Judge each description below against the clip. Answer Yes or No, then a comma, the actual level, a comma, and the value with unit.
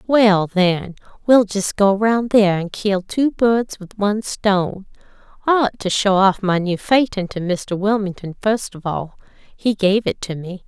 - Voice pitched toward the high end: Yes, high, 200 Hz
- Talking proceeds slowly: No, average, 185 wpm